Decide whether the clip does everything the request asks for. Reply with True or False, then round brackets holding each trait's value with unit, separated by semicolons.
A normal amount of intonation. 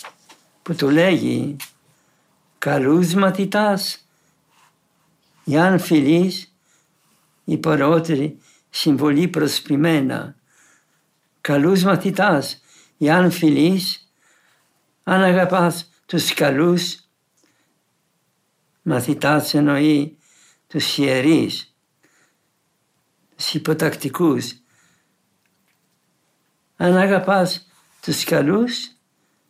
True (3.4 semitones)